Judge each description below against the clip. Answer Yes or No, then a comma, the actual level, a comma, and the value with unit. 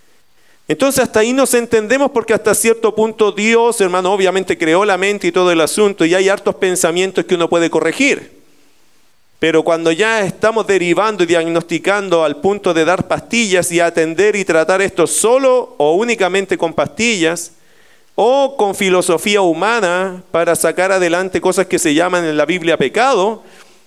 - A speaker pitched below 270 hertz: Yes, high, 190 Hz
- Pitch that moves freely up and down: No, average, 4.1 semitones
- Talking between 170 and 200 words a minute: No, average, 160 wpm